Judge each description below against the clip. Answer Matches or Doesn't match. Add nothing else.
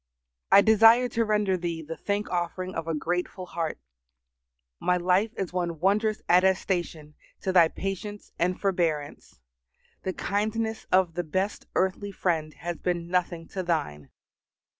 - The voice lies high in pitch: Doesn't match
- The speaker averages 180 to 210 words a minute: Doesn't match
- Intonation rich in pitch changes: Doesn't match